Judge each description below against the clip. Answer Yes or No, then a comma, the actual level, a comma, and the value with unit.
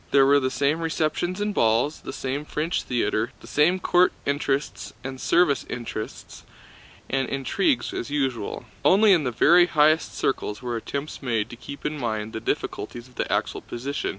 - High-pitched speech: No, medium, 140 Hz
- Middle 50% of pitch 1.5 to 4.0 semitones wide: No, average, 4.4 semitones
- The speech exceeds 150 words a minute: Yes, average, 175 wpm